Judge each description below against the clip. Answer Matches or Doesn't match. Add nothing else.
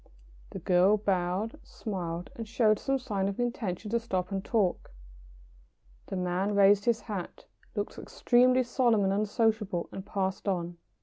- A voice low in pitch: Doesn't match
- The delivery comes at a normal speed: Matches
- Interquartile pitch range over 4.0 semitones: Doesn't match